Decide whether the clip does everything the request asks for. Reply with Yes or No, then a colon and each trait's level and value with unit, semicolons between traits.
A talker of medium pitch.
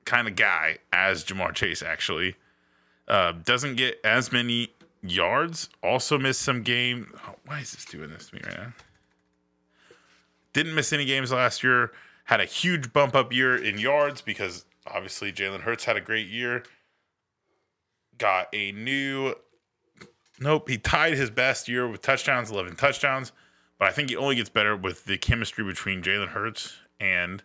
No: low, 120 Hz